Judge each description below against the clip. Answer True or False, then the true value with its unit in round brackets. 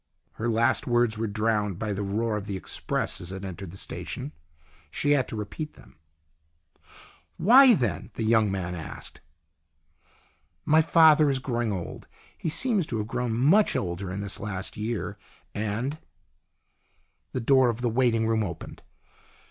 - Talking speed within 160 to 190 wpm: True (170 wpm)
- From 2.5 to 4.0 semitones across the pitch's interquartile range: False (4.5 semitones)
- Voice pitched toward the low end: True (110 Hz)